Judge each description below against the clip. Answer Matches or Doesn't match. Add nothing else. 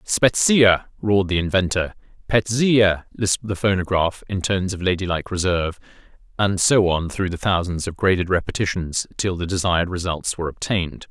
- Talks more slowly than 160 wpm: Matches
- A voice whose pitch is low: Matches